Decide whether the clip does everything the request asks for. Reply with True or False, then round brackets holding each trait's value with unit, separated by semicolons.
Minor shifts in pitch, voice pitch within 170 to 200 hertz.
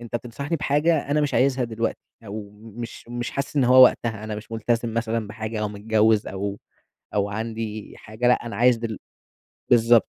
False (2.2 semitones; 115 Hz)